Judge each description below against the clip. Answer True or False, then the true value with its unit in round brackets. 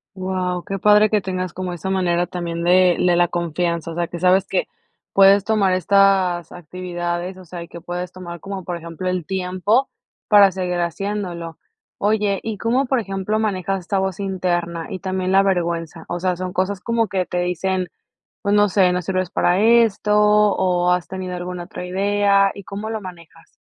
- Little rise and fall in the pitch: True (2.0 semitones)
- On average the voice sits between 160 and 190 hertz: True (185 Hz)